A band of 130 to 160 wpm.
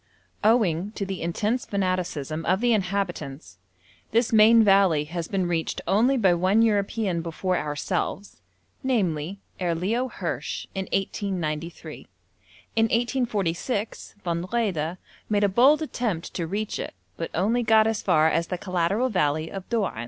Yes: average, 145 wpm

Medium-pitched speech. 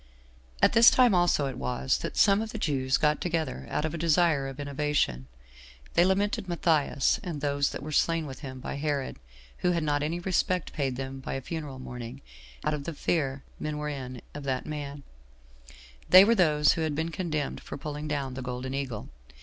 Yes: medium, 150 Hz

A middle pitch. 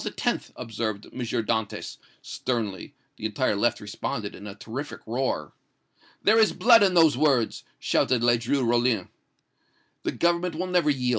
No: low, 120 Hz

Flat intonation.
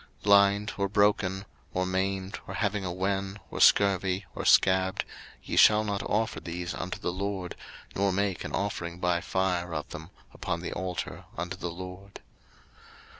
Yes: narrow, 1.8 semitones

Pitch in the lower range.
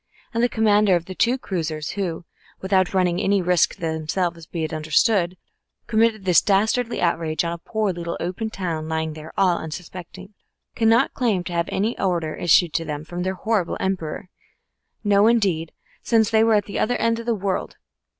No: medium, 185 Hz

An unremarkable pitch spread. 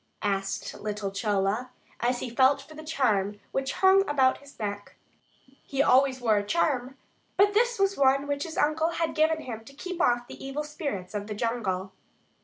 No: wide, 6.3 semitones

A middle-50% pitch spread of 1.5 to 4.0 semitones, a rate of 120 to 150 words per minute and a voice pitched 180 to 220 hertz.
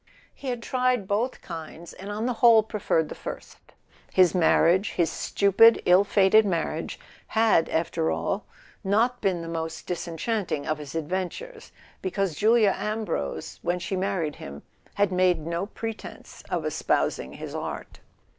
No: average, 4.7 semitones; average, 145 wpm; high, 190 Hz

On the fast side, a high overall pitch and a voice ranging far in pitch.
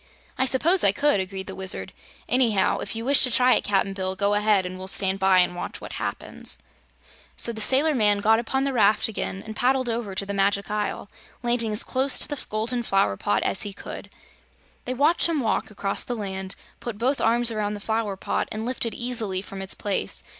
No: fast, 220 wpm; high, 215 Hz; average, 4.0 semitones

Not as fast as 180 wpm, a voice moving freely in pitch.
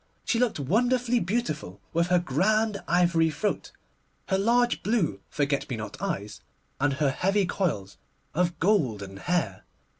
Yes: average, 140 wpm; wide, 7.2 semitones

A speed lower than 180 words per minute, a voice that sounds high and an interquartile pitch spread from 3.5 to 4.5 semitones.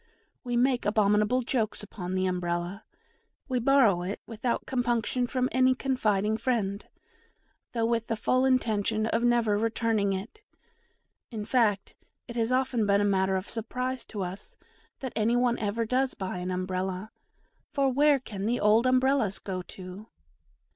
Yes: average, 155 wpm; high, 225 Hz; average, 3.9 semitones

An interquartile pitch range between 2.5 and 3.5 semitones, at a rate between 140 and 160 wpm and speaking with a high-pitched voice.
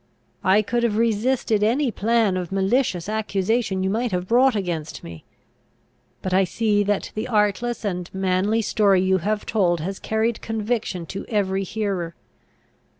Yes: average, 3.0 semitones; average, 150 wpm; high, 205 Hz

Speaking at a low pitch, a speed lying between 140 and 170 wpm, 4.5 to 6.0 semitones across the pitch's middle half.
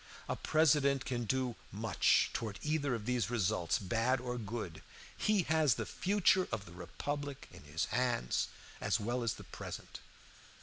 Yes: low, 125 Hz; average, 160 wpm; average, 5.2 semitones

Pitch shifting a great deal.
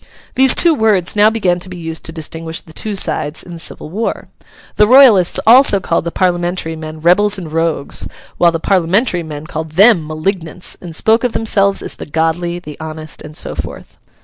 No: average, 4.2 semitones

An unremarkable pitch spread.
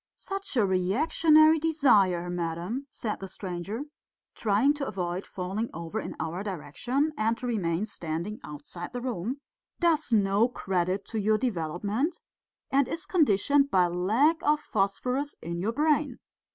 No: wide, 7.5 semitones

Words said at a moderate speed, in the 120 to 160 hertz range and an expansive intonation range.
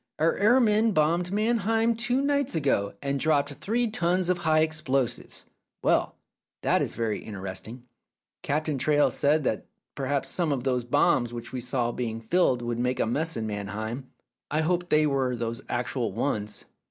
Yes: average, 165 wpm; medium, 140 Hz; wide, 6.5 semitones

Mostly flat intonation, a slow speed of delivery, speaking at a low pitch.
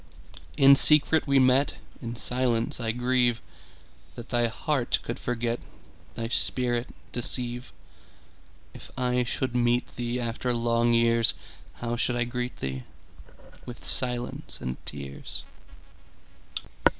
Yes: narrow, 1.2 semitones; slow, 90 wpm; low, 120 Hz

